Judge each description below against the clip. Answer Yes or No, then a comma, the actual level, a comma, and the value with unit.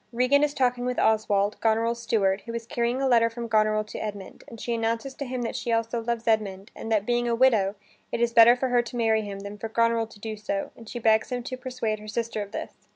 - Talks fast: Yes, fast, 255 wpm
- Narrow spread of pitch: Yes, narrow, 2.0 semitones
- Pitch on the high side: Yes, high, 230 Hz